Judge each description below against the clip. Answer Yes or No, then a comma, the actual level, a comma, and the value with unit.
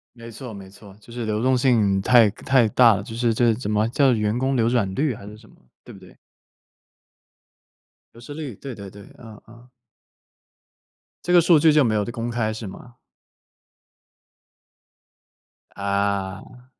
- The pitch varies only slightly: No, average, 3.2 semitones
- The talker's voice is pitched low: Yes, low, 115 Hz